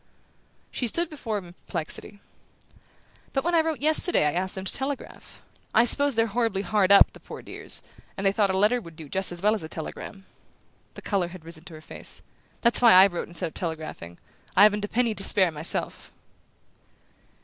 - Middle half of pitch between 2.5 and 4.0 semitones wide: No, average, 5.1 semitones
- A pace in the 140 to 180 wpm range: No, average, 200 wpm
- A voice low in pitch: No, high, 200 Hz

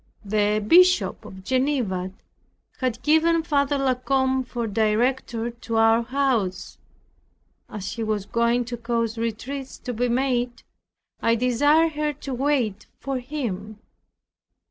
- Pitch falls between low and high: No, high, 245 Hz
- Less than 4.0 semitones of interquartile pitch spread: Yes, average, 3.4 semitones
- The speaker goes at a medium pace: No, slow, 125 wpm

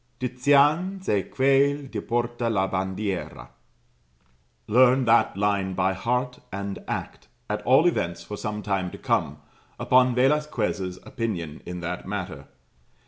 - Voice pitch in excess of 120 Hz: No, low, 110 Hz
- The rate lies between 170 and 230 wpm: No, slow, 135 wpm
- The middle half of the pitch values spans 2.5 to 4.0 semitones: No, average, 5.2 semitones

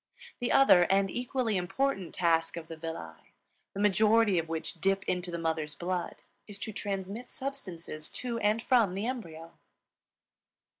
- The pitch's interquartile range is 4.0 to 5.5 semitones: Yes, average, 5.2 semitones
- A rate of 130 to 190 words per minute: Yes, average, 150 wpm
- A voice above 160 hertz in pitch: Yes, high, 190 Hz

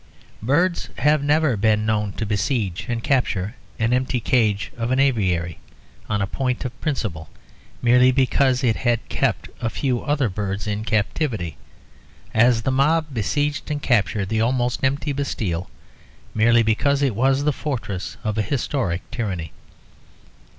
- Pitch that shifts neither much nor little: Yes, average, 4.3 semitones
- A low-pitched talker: Yes, low, 120 Hz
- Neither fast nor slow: Yes, average, 150 wpm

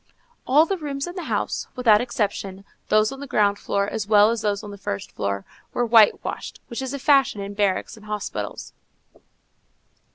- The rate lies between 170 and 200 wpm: Yes, average, 190 wpm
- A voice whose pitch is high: Yes, high, 215 Hz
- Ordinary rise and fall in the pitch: Yes, average, 4.6 semitones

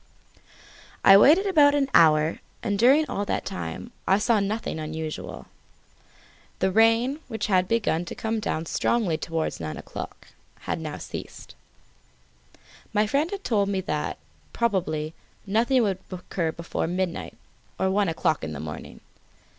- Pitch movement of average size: No, wide, 6.0 semitones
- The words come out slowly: No, average, 145 wpm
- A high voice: Yes, high, 195 Hz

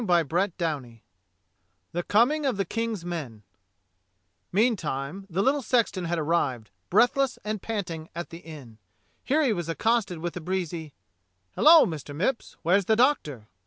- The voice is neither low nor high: Yes, medium, 175 Hz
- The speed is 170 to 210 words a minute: No, average, 145 wpm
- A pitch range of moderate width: No, wide, 6.1 semitones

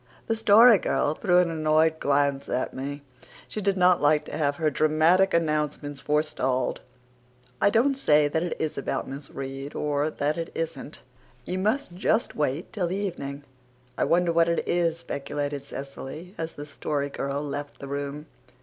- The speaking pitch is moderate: Yes, medium, 155 Hz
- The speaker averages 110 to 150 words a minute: No, average, 170 wpm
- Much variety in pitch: No, average, 3.6 semitones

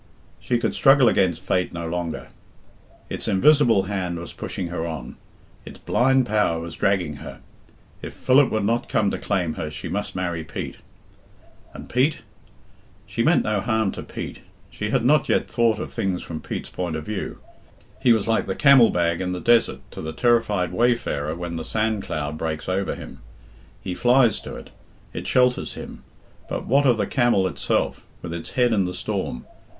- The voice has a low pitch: Yes, low, 100 Hz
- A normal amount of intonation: No, wide, 5.7 semitones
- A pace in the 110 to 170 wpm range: No, average, 185 wpm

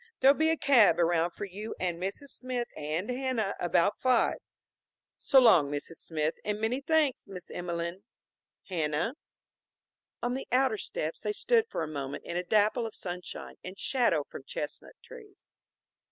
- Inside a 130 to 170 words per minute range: Yes, average, 160 wpm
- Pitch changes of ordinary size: No, wide, 7.1 semitones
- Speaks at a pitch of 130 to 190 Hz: No, high, 205 Hz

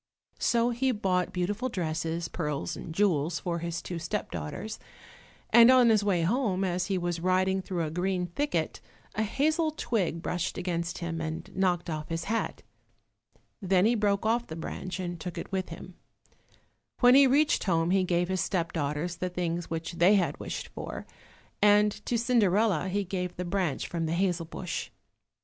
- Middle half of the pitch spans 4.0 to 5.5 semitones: No, average, 3.4 semitones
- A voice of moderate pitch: Yes, medium, 180 Hz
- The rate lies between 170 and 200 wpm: Yes, average, 175 wpm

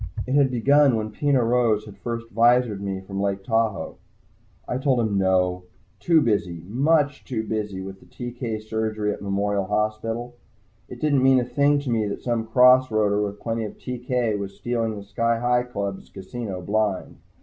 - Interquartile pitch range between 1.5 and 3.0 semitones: No, average, 3.4 semitones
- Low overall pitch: Yes, low, 110 Hz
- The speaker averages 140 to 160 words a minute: No, average, 180 wpm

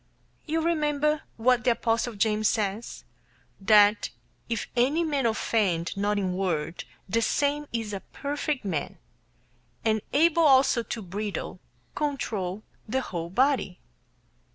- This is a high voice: Yes, high, 225 Hz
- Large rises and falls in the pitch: Yes, wide, 5.9 semitones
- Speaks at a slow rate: Yes, slow, 125 wpm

